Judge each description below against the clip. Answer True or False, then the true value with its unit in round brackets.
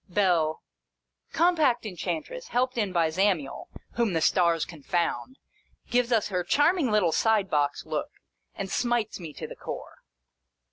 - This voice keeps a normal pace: True (145 wpm)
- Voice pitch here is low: False (205 Hz)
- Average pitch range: False (6.3 semitones)